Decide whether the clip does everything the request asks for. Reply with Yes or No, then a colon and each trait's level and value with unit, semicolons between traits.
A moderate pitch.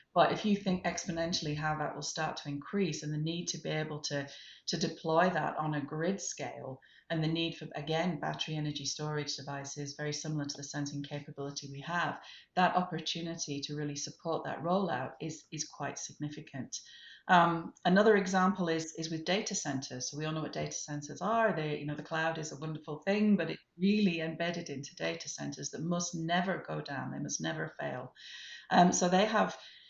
Yes: medium, 155 Hz